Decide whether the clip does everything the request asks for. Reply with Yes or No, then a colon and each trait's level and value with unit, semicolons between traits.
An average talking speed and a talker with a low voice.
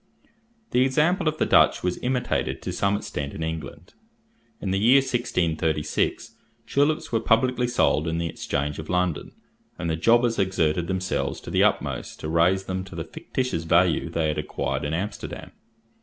Yes: average, 170 wpm; very low, 95 Hz